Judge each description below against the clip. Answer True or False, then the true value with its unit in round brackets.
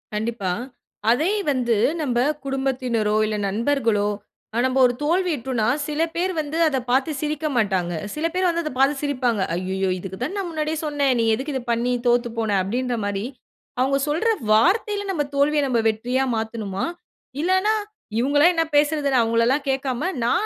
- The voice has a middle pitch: False (265 Hz)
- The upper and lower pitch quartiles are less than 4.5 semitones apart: False (4.8 semitones)